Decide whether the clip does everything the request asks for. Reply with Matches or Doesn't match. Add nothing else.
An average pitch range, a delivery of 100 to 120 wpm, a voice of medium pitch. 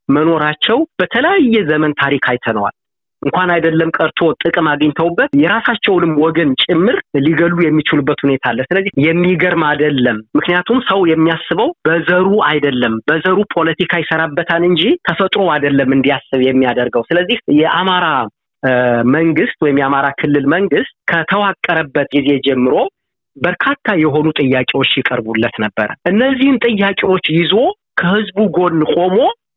Matches